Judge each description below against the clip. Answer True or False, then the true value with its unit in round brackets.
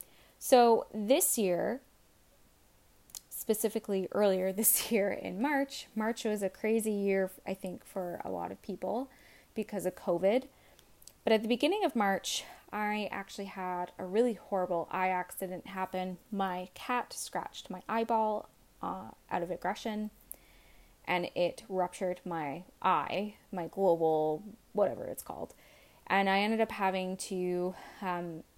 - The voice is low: False (195 Hz)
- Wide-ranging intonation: False (3.3 semitones)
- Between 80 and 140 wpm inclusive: True (135 wpm)